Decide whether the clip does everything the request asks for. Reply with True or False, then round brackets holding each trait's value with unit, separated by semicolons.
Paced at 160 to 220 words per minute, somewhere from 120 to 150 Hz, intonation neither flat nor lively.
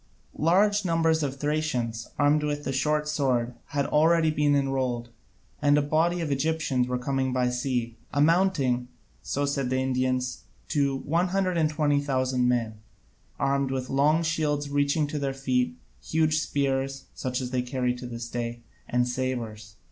False (150 wpm; 140 Hz; 3.3 semitones)